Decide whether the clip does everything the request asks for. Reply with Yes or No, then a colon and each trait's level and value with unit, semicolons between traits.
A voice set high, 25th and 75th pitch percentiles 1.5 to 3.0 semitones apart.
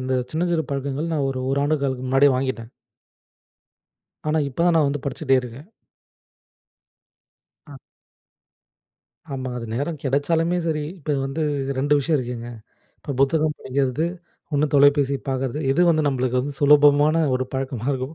No: medium, 140 Hz; narrow, 2.6 semitones